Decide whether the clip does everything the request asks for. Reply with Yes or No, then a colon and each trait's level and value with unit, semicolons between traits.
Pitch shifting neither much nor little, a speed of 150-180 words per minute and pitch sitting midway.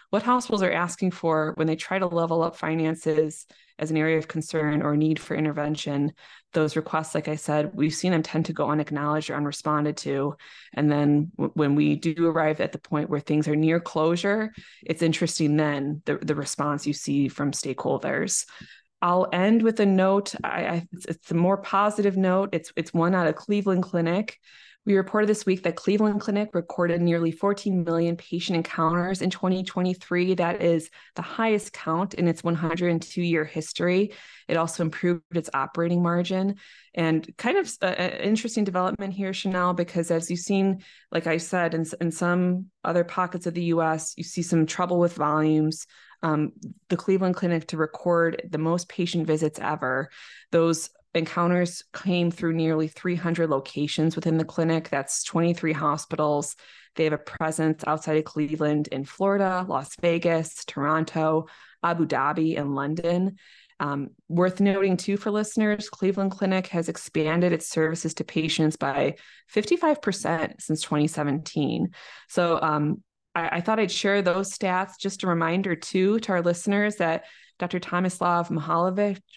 Yes: average, 3.0 semitones; average, 165 wpm; medium, 170 Hz